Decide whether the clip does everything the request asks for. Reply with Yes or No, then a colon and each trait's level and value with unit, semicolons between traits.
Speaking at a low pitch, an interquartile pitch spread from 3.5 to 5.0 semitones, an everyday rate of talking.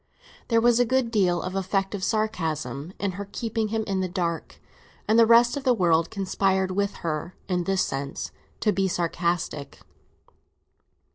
No: high, 195 Hz; average, 4.1 semitones; average, 160 wpm